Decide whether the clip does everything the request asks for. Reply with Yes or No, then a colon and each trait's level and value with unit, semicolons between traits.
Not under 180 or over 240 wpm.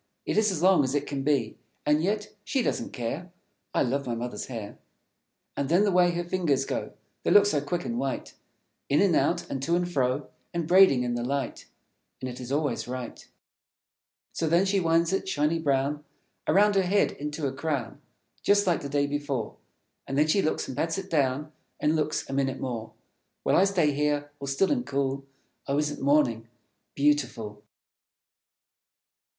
Yes: average, 185 wpm